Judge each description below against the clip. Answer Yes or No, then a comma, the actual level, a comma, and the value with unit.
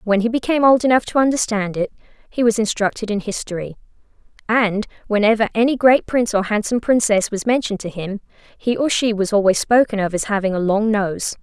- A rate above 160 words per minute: Yes, average, 195 wpm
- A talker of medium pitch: No, high, 215 Hz